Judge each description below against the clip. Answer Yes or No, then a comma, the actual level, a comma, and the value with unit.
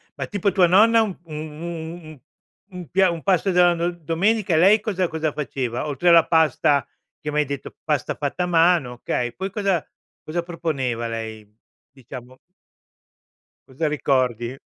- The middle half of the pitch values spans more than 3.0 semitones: Yes, average, 4.9 semitones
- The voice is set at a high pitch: No, medium, 160 Hz